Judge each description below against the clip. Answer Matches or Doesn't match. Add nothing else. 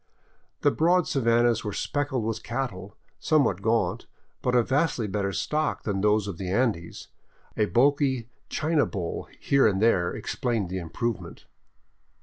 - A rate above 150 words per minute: Doesn't match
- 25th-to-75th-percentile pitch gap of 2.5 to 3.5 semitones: Doesn't match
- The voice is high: Doesn't match